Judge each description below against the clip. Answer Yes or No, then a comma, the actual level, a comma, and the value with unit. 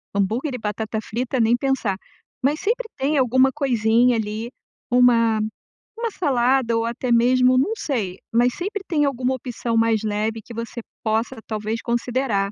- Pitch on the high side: Yes, high, 240 Hz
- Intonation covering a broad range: No, average, 2.9 semitones